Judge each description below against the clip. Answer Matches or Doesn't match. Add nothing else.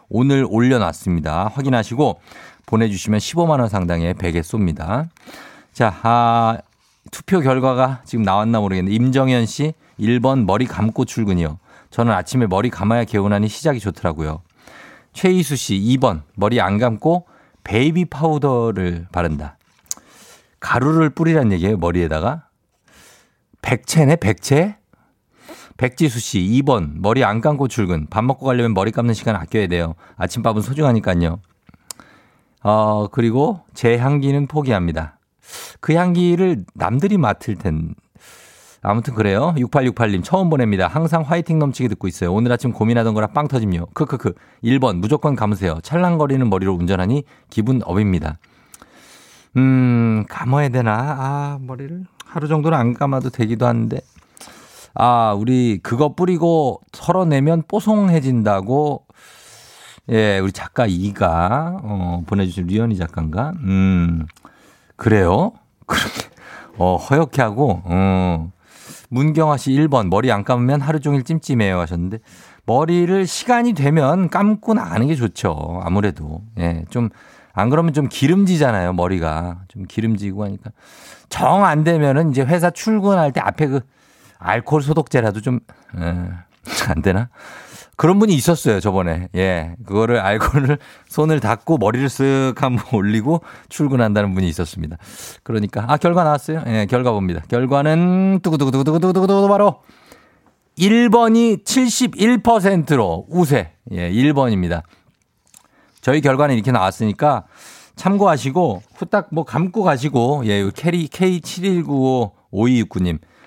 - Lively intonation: Matches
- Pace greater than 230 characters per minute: Matches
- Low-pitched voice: Matches